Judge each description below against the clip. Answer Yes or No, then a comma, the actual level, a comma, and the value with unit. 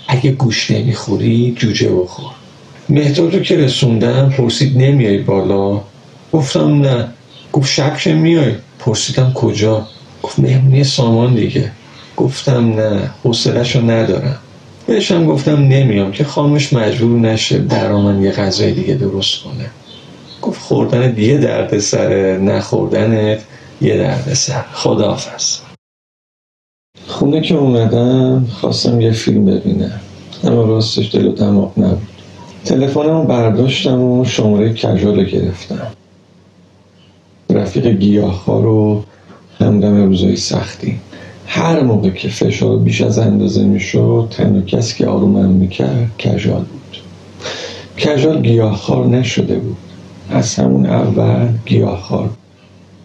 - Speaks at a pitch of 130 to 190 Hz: No, low, 115 Hz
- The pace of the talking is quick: No, average, 120 wpm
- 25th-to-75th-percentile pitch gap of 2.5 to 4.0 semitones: No, average, 4.8 semitones